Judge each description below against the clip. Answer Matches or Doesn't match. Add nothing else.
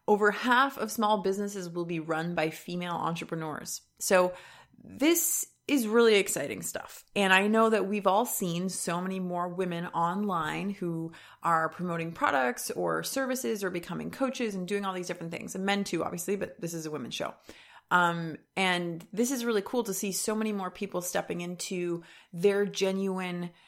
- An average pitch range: Matches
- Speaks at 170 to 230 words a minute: Matches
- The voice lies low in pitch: Doesn't match